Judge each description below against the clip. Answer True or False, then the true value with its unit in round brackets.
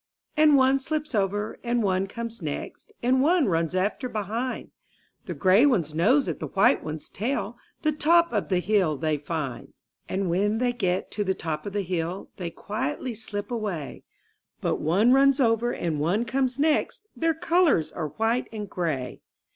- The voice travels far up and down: True (6.5 semitones)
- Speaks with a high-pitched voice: True (210 Hz)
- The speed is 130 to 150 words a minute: False (180 wpm)